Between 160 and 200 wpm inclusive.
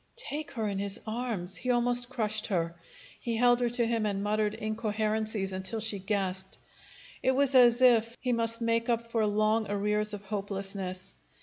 Yes: average, 175 wpm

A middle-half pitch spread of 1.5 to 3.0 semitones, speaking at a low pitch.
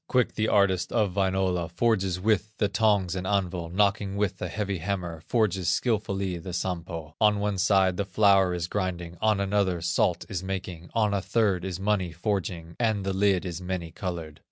Yes: narrow, 2.5 semitones; very low, 95 Hz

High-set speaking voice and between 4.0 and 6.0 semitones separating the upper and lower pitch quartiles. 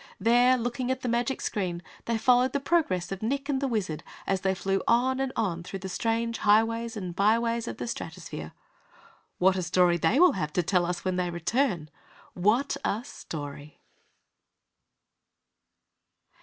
Yes: high, 215 Hz; average, 5.2 semitones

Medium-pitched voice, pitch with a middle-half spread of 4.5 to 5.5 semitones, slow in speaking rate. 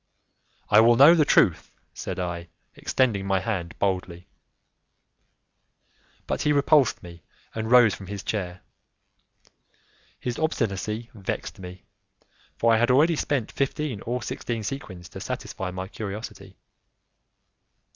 No: low, 110 Hz; average, 5.1 semitones; slow, 125 wpm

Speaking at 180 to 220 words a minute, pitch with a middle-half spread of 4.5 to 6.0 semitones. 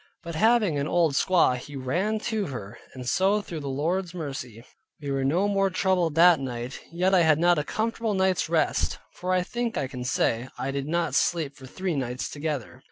Yes: fast, 205 wpm; wide, 5.5 semitones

